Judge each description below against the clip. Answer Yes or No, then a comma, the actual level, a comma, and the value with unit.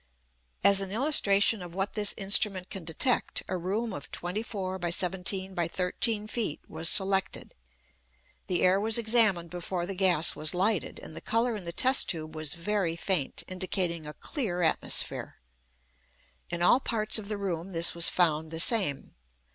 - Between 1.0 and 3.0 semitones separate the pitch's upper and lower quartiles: No, average, 3.5 semitones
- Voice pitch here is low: No, medium, 185 Hz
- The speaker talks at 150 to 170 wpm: Yes, average, 165 wpm